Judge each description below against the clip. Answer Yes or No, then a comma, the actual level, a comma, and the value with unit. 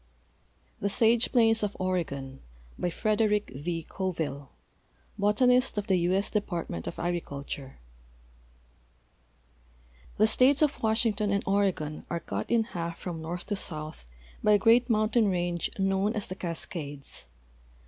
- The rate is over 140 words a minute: No, slow, 135 wpm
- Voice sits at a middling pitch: No, high, 195 Hz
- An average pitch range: Yes, average, 4.5 semitones